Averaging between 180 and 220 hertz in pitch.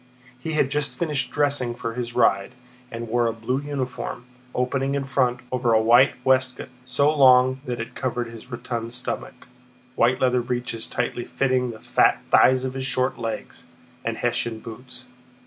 No: low, 125 Hz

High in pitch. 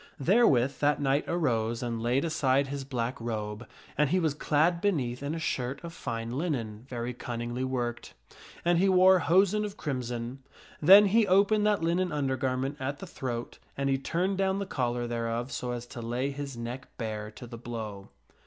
No: low, 135 Hz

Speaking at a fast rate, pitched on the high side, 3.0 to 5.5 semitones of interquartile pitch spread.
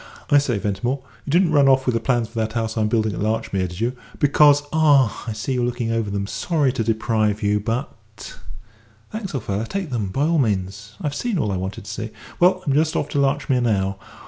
No: fast, 230 wpm; low, 115 Hz; average, 4.9 semitones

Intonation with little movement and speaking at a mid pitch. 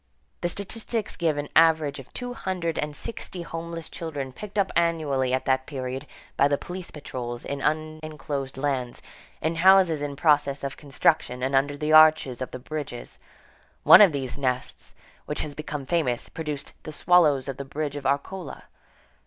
No: average, 3.5 semitones; medium, 150 Hz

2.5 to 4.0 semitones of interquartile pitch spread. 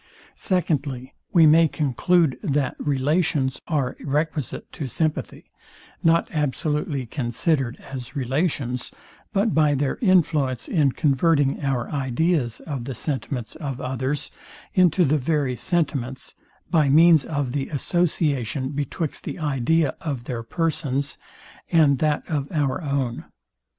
Yes: average, 3.5 semitones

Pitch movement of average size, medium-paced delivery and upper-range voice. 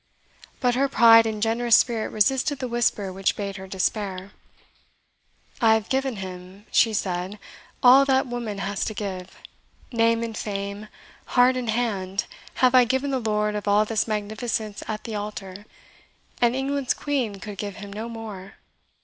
Yes: average, 3.3 semitones; average, 160 wpm; high, 215 Hz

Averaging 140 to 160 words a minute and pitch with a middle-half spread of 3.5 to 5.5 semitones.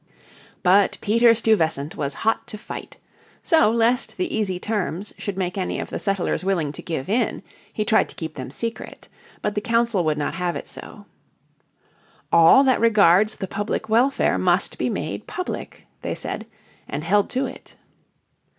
No: average, 170 wpm; average, 4.5 semitones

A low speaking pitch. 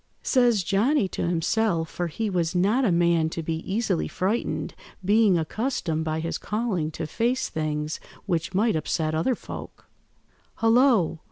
No: medium, 180 Hz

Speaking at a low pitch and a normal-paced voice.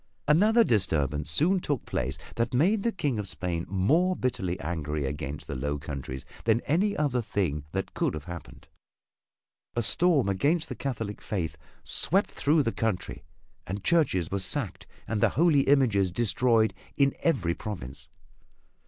Yes: low, 110 Hz; average, 155 wpm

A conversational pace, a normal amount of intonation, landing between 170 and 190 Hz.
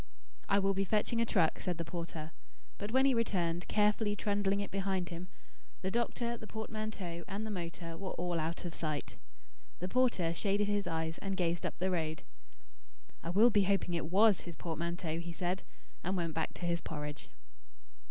Yes: average, 185 wpm; average, 3.5 semitones; medium, 185 Hz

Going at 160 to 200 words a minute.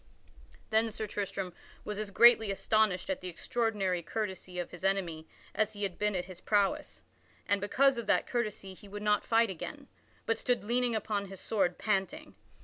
Yes: average, 180 wpm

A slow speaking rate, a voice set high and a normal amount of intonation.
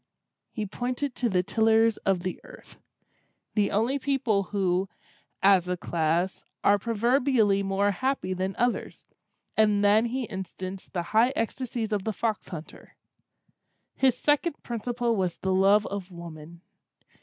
Yes: slow, 130 wpm; high, 205 Hz; average, 3.9 semitones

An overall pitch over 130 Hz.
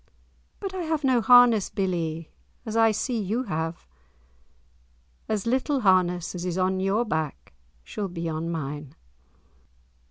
Yes: high, 190 Hz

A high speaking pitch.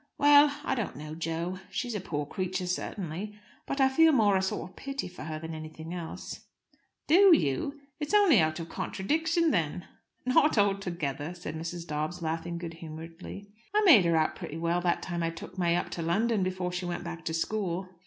No: medium, 180 Hz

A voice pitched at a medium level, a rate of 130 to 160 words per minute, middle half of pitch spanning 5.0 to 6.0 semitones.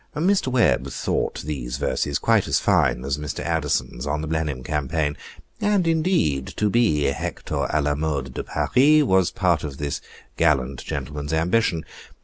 No: very low, 75 Hz; average, 155 wpm; wide, 5.4 semitones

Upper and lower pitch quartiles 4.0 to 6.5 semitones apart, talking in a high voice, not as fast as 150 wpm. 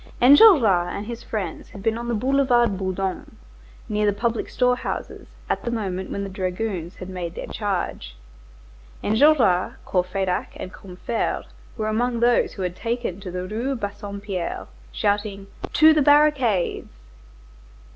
Yes: average, 4.3 semitones; high, 205 Hz; average, 140 wpm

